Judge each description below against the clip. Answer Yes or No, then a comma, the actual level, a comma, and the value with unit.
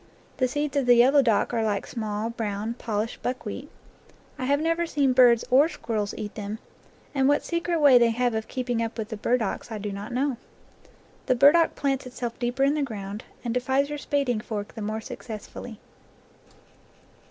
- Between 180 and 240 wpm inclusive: Yes, average, 190 wpm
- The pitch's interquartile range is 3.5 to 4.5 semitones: Yes, average, 3.9 semitones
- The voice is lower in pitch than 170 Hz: No, high, 245 Hz